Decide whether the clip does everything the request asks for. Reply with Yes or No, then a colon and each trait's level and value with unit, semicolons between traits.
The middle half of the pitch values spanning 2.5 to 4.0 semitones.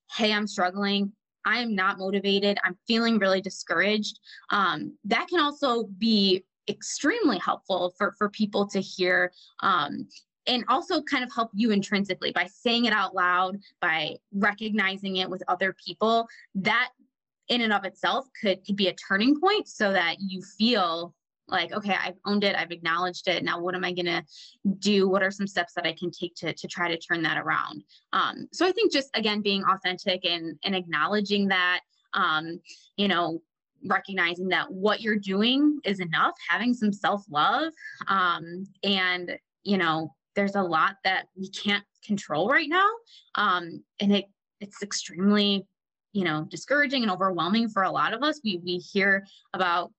Yes: average, 3.0 semitones